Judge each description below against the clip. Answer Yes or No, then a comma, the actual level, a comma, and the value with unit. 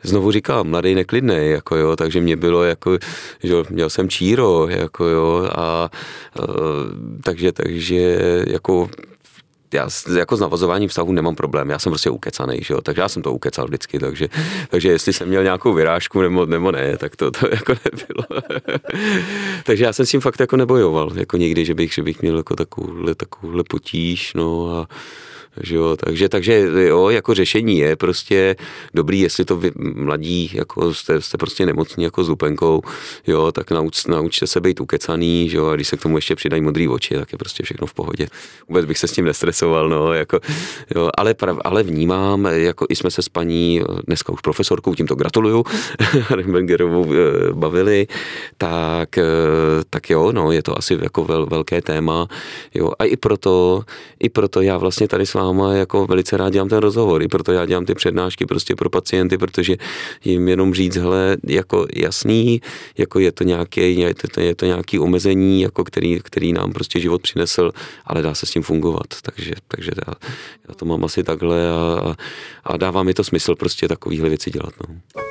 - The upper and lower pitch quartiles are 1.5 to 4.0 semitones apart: Yes, narrow, 2.4 semitones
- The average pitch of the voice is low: Yes, very low, 90 Hz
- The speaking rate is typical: No, fast, 185 wpm